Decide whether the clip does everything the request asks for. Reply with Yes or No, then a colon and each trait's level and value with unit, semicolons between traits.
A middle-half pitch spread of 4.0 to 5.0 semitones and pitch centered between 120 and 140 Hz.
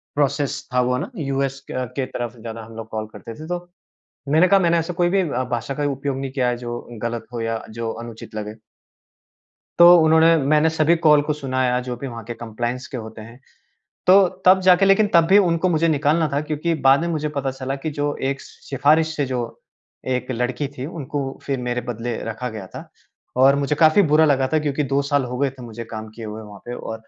Yes: average, 4.6 semitones; low, 135 Hz